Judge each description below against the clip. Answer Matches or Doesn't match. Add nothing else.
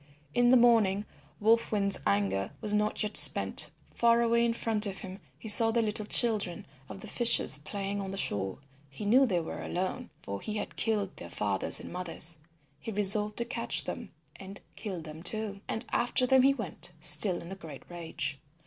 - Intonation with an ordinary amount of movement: Matches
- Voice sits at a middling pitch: Doesn't match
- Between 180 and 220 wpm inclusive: Matches